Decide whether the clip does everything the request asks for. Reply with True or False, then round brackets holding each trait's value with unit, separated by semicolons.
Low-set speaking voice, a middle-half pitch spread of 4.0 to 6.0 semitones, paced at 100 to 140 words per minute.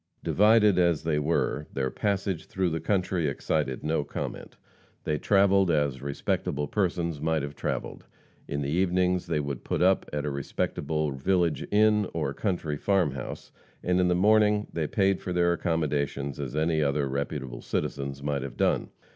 False (80 Hz; 4.4 semitones; 165 wpm)